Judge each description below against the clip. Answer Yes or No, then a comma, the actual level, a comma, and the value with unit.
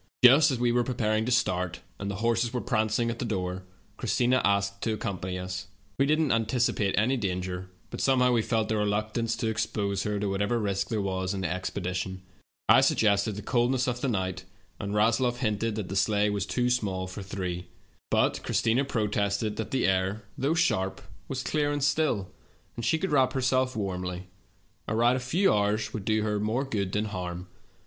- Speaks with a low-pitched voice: Yes, low, 110 Hz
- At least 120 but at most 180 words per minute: No, average, 200 wpm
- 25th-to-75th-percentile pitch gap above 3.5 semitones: Yes, average, 4.0 semitones